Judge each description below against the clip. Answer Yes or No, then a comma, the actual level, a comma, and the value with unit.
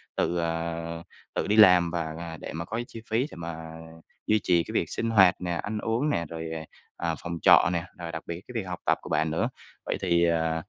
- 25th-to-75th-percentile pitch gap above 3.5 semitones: No, average, 2.8 semitones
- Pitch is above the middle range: No, very low, 85 Hz